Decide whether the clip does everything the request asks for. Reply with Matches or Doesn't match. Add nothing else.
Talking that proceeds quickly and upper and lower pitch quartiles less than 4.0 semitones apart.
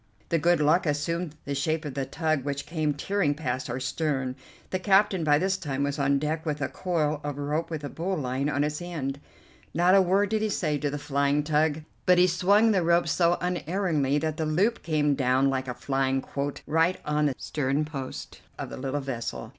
Matches